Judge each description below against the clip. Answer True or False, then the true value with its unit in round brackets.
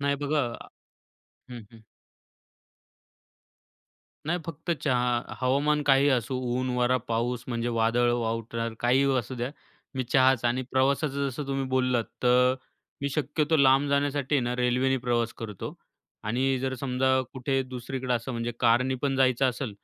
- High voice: False (130 Hz)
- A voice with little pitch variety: True (2.1 semitones)